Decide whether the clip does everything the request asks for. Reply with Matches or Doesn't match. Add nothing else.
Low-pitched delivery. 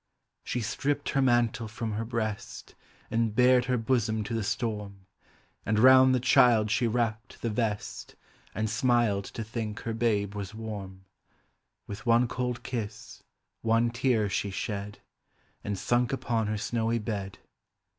Matches